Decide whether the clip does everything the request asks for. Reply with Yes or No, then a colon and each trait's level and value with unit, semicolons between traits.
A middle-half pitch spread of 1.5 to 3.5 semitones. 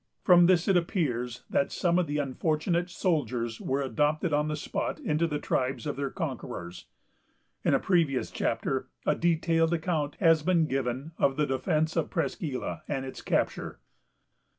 No: average, 3.9 semitones